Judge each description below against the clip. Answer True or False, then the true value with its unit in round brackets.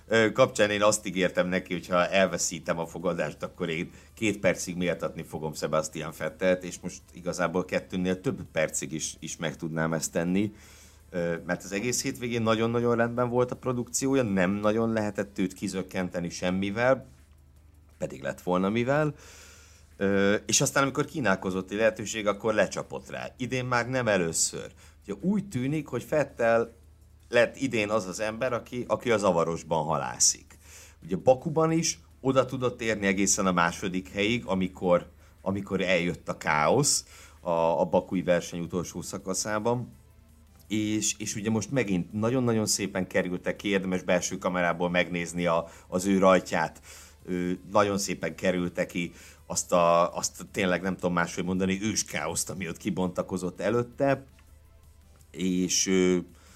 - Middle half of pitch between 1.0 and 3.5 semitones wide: False (4.2 semitones)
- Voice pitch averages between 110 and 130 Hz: False (95 Hz)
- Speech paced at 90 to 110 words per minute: False (145 wpm)